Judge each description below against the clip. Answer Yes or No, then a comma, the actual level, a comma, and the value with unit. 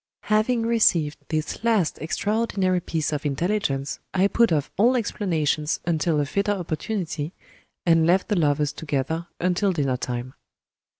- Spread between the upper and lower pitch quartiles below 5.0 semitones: No, wide, 5.4 semitones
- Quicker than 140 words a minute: No, slow, 135 wpm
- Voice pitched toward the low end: No, medium, 170 Hz